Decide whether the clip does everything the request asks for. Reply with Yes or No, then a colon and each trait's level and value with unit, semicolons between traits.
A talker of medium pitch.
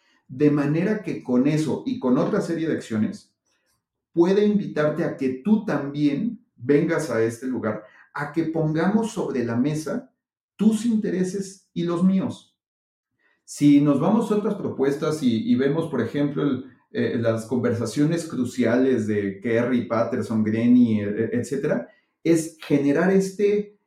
Yes: medium, 150 Hz